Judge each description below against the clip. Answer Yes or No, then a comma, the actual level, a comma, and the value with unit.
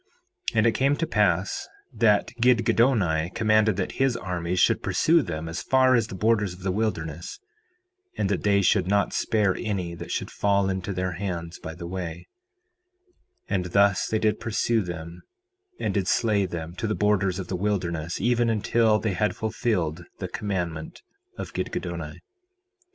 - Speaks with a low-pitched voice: Yes, low, 100 Hz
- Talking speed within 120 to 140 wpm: No, average, 165 wpm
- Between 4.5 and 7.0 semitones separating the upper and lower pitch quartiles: No, average, 3.8 semitones